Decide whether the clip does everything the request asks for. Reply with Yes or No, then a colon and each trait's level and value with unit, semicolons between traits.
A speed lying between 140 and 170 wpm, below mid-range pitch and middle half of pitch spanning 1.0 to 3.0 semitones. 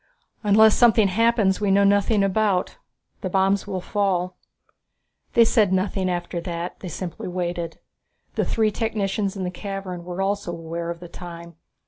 No: average, 160 wpm; high, 190 Hz; narrow, 2.5 semitones